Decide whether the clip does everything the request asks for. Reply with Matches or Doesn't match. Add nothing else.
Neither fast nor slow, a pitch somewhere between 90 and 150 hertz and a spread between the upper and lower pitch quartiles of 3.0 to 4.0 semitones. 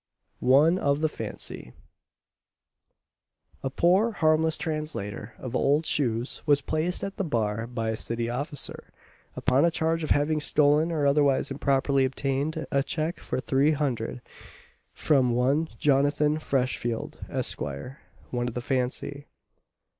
Doesn't match